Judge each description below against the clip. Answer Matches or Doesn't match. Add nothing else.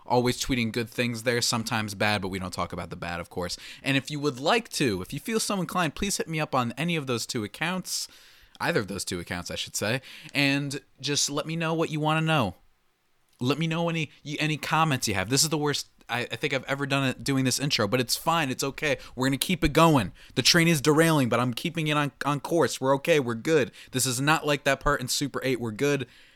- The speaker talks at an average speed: Doesn't match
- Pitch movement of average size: Matches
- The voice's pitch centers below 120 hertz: Doesn't match